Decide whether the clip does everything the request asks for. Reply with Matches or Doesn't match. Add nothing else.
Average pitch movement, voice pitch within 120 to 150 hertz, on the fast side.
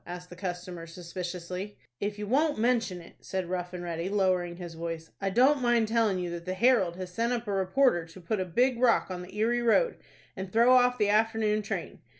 Doesn't match